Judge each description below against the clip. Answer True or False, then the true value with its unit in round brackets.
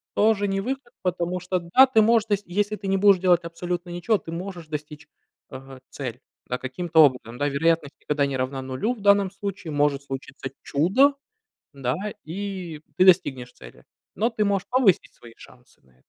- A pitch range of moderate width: False (6.2 semitones)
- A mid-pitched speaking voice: True (175 Hz)